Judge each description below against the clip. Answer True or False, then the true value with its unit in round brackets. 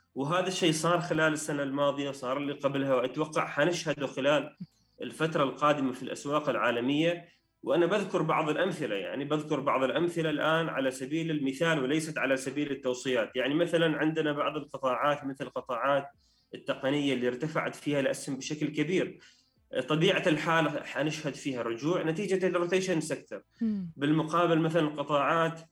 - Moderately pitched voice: True (150 Hz)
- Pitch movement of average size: True (3.2 semitones)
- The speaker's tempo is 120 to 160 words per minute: True (135 wpm)